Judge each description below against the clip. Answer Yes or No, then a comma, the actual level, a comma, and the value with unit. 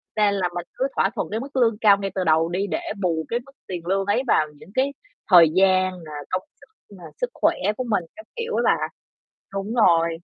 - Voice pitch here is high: Yes, high, 195 Hz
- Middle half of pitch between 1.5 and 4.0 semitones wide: No, average, 4.4 semitones